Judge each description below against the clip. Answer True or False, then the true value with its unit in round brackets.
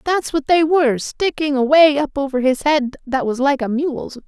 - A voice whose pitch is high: True (285 Hz)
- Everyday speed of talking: False (210 wpm)